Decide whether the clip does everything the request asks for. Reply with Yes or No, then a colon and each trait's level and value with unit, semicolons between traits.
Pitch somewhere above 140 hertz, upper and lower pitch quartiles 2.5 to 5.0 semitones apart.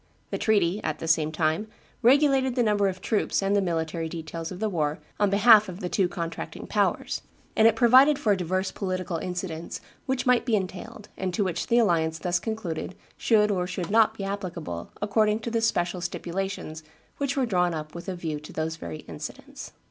Yes: medium, 185 Hz; average, 4.4 semitones